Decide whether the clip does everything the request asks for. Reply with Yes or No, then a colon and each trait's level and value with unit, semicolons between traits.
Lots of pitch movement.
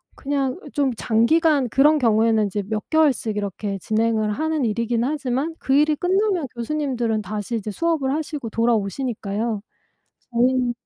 No: average, 5.0 semitones